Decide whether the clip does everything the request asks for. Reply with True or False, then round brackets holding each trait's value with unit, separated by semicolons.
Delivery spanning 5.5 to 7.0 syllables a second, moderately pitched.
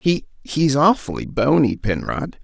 False (3.8 syllables/s; 150 Hz)